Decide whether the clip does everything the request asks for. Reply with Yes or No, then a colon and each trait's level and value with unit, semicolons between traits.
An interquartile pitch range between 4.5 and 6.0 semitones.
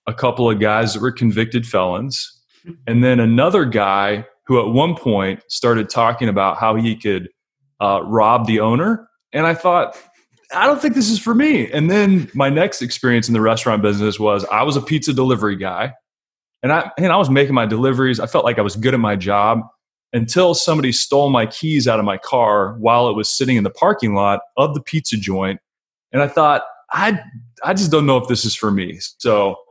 Yes: wide, 5.4 semitones